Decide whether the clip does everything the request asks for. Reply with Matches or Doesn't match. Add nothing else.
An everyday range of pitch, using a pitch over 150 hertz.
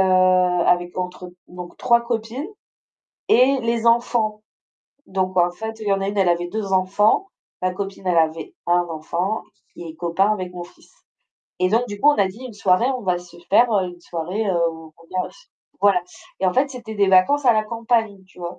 Matches